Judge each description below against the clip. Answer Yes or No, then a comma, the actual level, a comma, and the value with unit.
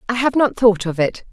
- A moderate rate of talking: No, fast, 275 wpm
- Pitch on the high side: Yes, high, 220 Hz